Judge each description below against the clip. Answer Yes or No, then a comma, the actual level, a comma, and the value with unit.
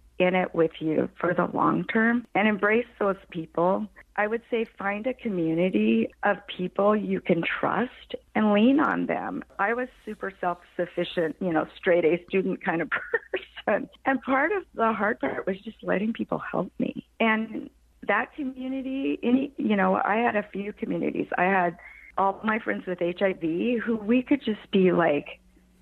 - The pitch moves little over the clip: No, average, 4.8 semitones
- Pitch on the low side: No, high, 205 Hz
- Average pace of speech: Yes, average, 175 wpm